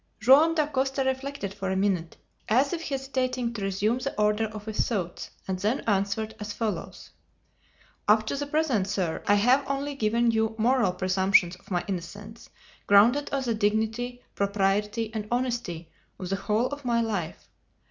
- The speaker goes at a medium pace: Yes, average, 165 wpm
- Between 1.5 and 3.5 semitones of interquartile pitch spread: No, average, 4.3 semitones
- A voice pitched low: No, high, 220 Hz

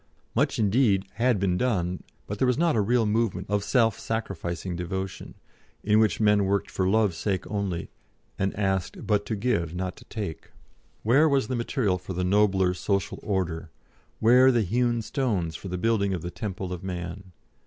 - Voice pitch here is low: Yes, low, 100 Hz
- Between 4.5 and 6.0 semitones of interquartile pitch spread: No, average, 3.5 semitones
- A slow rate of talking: No, average, 180 wpm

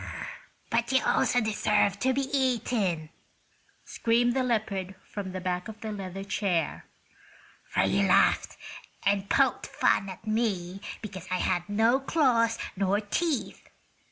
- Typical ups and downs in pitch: Yes, average, 3.9 semitones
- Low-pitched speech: No, high, 205 Hz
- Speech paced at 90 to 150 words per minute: Yes, slow, 135 wpm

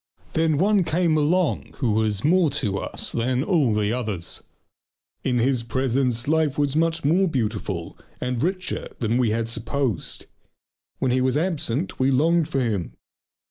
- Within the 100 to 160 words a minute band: Yes, average, 155 wpm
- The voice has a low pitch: Yes, low, 130 Hz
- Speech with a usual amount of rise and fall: No, wide, 5.7 semitones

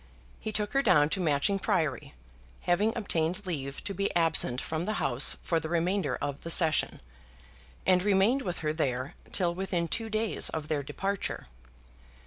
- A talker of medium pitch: Yes, medium, 175 Hz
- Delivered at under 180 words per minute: Yes, average, 165 wpm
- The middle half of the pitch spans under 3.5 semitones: No, average, 4.4 semitones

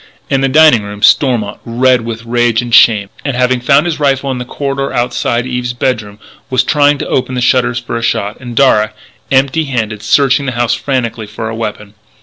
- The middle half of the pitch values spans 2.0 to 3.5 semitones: Yes, average, 2.8 semitones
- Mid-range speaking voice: No, low, 125 Hz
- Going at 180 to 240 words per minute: Yes, average, 200 wpm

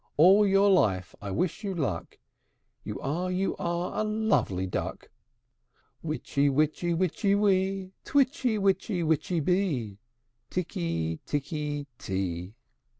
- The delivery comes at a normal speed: No, slow, 115 wpm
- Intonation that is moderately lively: No, wide, 7.8 semitones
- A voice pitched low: No, medium, 170 Hz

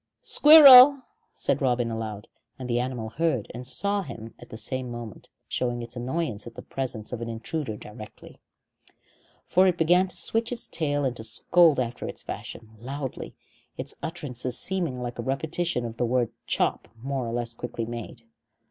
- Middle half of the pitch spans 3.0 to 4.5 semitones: No, wide, 5.6 semitones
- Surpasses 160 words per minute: Yes, average, 170 wpm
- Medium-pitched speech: No, low, 125 Hz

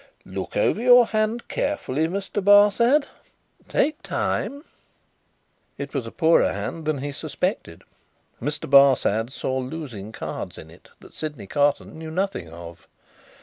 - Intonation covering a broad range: Yes, wide, 7.6 semitones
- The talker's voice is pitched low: No, medium, 155 Hz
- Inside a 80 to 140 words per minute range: Yes, slow, 135 wpm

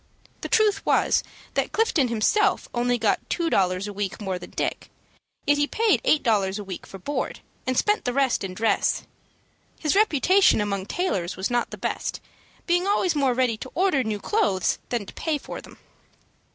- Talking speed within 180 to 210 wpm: Yes, average, 185 wpm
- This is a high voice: Yes, very high, 250 Hz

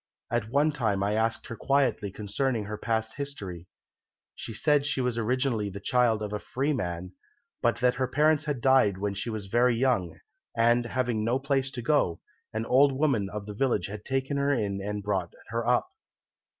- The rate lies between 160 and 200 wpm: Yes, average, 195 wpm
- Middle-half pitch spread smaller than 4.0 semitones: No, average, 4.3 semitones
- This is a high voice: No, low, 115 Hz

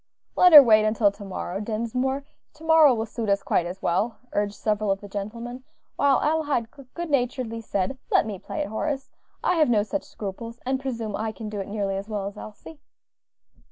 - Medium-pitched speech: No, high, 225 Hz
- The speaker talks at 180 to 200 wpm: Yes, average, 195 wpm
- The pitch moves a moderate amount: Yes, average, 4.6 semitones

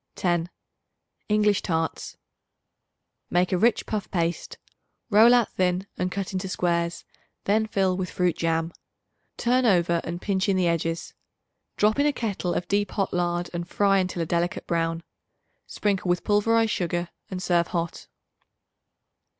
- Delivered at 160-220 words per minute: No, average, 150 wpm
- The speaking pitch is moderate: Yes, medium, 180 Hz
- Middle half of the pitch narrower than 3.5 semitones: Yes, average, 3.0 semitones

